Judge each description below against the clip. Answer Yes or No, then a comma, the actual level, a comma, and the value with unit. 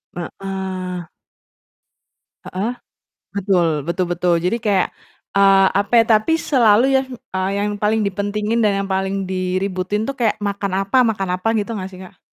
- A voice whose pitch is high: Yes, high, 195 Hz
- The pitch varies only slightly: Yes, narrow, 2.2 semitones